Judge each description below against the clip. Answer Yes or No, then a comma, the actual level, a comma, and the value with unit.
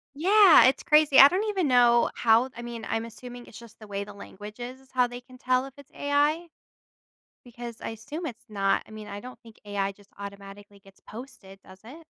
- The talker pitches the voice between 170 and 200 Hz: No, high, 240 Hz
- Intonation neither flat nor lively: Yes, average, 4.4 semitones